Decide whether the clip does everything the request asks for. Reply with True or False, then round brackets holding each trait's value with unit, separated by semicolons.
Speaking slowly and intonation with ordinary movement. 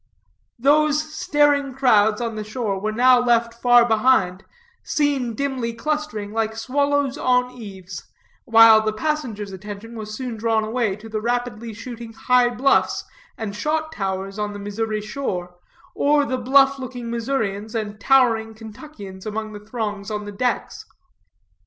False (145 wpm; 3.5 semitones)